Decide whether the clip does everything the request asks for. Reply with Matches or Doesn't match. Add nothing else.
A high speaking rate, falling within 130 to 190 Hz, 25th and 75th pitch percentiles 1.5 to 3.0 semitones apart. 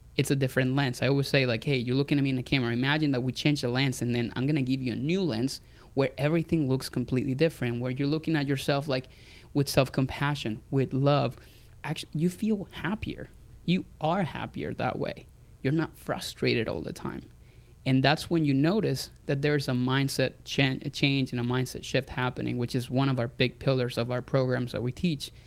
Matches